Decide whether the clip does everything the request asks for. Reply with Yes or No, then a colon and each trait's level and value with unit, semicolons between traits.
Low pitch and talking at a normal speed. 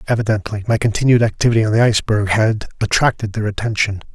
Yes: low, 110 Hz; average, 160 wpm